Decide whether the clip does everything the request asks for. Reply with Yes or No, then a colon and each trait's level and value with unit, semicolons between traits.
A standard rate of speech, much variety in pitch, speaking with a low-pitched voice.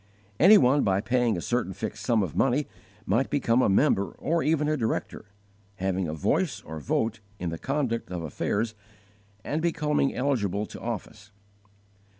Yes: average, 160 wpm; wide, 6.5 semitones; low, 115 Hz